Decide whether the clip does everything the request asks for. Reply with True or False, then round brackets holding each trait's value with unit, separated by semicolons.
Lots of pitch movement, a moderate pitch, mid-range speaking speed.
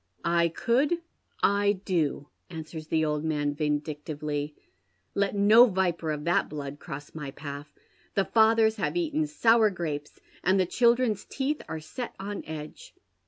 True (6.5 semitones; 170 Hz; 150 wpm)